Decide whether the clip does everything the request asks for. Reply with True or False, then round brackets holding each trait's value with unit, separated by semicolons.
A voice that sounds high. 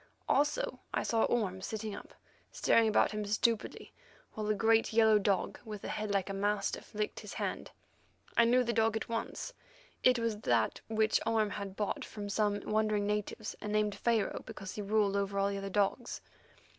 True (210 Hz)